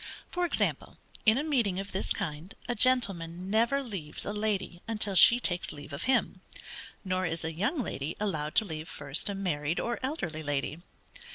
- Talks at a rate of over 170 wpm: Yes, average, 180 wpm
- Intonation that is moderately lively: No, wide, 5.9 semitones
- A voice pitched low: No, high, 190 Hz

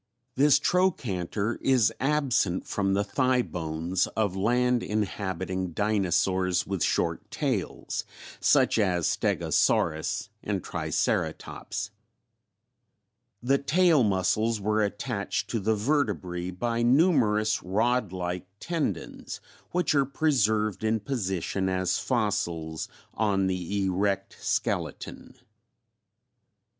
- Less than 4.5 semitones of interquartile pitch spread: No, average, 4.8 semitones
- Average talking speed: No, slow, 100 wpm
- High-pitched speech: No, low, 105 Hz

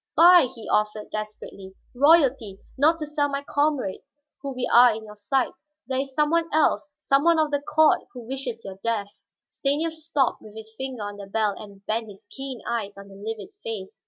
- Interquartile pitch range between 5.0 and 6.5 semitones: Yes, wide, 5.4 semitones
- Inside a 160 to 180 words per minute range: No, average, 200 wpm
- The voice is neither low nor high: No, very high, 250 Hz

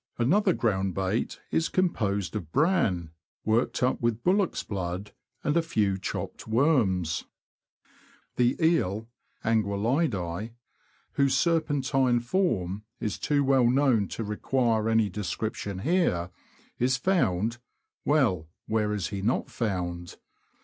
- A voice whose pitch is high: No, low, 115 Hz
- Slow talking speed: Yes, slow, 120 wpm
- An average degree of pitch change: No, wide, 5.9 semitones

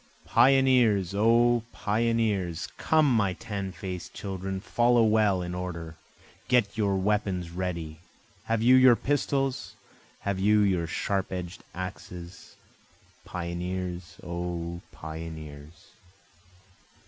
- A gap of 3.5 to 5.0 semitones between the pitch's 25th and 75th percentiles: Yes, average, 4.3 semitones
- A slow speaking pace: Yes, slow, 100 wpm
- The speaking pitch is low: Yes, very low, 95 Hz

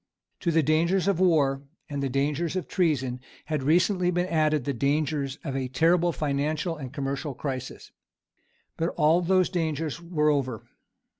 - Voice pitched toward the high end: No, medium, 155 Hz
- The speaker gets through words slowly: No, average, 155 wpm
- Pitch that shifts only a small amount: No, average, 3.6 semitones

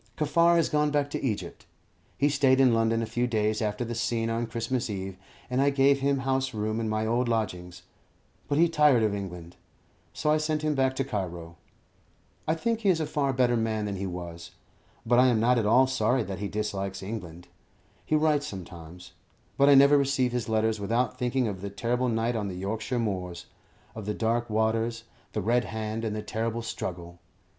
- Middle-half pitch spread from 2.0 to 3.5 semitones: No, average, 4.1 semitones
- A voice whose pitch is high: No, low, 115 Hz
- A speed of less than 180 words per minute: No, average, 200 wpm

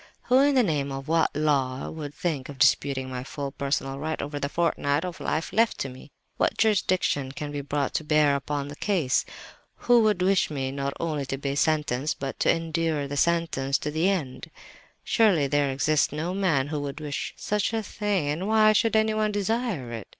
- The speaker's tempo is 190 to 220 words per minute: Yes, average, 195 wpm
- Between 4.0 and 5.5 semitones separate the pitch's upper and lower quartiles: Yes, average, 4.9 semitones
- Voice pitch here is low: No, medium, 150 Hz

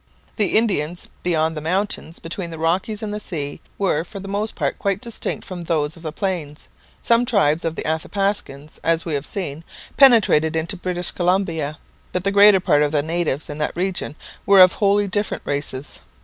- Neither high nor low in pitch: Yes, medium, 175 Hz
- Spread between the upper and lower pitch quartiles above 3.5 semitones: Yes, average, 4.2 semitones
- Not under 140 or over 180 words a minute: No, average, 190 wpm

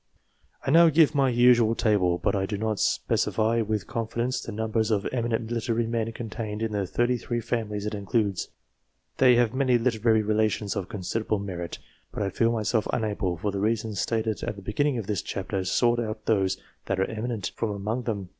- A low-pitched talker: Yes, low, 110 Hz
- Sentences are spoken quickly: Yes, fast, 210 wpm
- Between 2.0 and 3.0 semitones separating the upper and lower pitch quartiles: Yes, narrow, 2.4 semitones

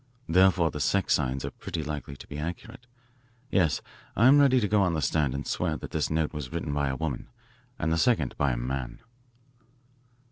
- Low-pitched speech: Yes, very low, 80 Hz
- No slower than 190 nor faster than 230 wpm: Yes, average, 200 wpm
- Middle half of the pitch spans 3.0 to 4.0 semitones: No, average, 5.0 semitones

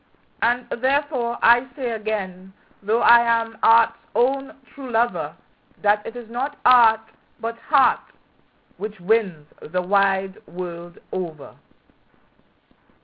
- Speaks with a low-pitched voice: No, high, 225 Hz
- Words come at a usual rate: No, slow, 115 wpm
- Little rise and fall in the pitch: No, average, 3.9 semitones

